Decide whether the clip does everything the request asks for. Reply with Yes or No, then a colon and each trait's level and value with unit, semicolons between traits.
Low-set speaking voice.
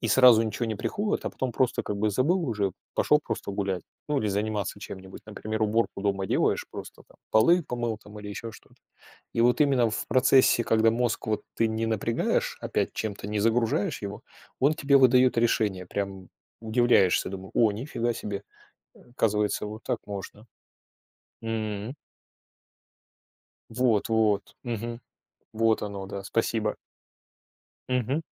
Yes: low, 110 Hz